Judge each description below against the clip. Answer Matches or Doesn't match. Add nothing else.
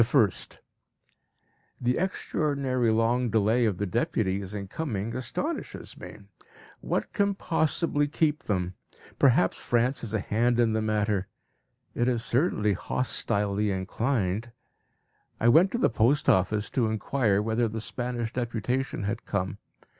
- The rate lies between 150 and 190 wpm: Doesn't match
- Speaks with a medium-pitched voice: Doesn't match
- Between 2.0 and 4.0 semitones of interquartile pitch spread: Matches